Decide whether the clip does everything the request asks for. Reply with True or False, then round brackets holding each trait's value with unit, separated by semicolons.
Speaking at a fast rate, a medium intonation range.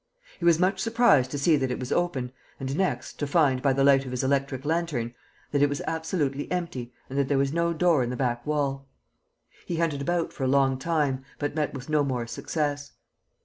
True (220 wpm; 3.5 semitones)